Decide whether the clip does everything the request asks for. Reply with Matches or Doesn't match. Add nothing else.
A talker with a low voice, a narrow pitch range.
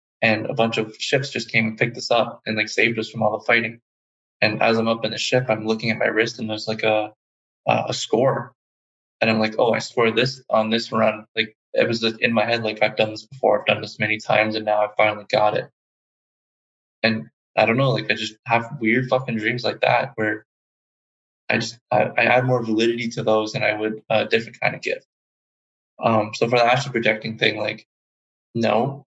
Matches